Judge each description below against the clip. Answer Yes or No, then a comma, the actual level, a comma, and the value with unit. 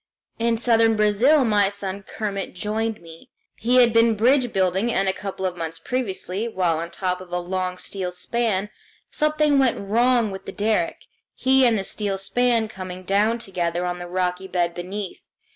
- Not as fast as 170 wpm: No, average, 175 wpm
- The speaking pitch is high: Yes, high, 200 Hz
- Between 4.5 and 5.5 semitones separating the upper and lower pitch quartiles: No, average, 3.9 semitones